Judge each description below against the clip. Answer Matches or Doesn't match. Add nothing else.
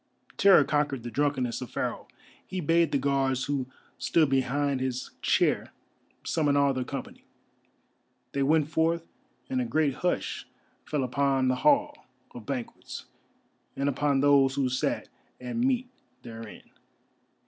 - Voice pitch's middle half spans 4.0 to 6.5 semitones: Doesn't match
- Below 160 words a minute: Matches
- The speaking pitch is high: Doesn't match